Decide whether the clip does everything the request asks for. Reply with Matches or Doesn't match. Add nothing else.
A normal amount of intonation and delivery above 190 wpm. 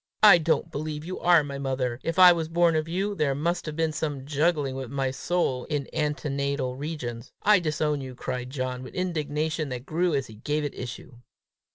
Matches